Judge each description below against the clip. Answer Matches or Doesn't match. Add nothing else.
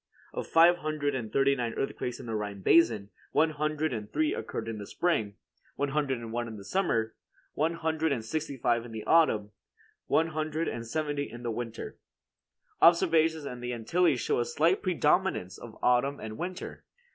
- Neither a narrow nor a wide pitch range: Doesn't match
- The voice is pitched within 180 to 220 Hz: Doesn't match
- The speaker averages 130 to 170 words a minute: Doesn't match